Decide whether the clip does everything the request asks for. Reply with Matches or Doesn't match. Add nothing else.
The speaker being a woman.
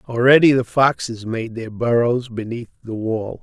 Doesn't match